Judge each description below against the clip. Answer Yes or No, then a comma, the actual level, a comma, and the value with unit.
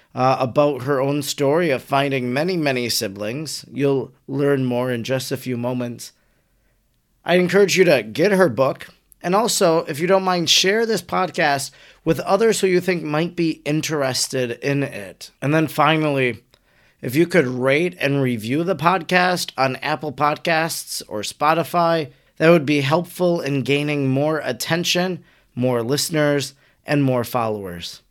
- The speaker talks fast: No, average, 155 wpm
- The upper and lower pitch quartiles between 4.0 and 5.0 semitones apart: Yes, average, 4.4 semitones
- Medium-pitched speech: Yes, medium, 145 Hz